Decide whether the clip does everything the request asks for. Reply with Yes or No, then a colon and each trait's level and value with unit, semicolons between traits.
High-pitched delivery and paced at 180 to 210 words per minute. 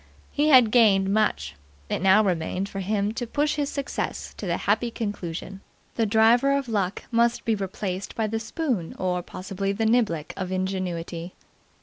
No: high, 205 Hz; average, 165 wpm